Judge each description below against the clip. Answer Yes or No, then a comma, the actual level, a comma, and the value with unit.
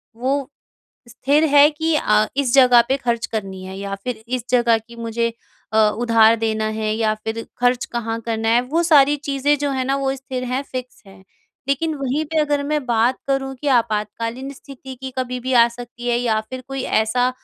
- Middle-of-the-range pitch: No, very high, 250 Hz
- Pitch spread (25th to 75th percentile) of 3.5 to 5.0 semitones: No, average, 3.1 semitones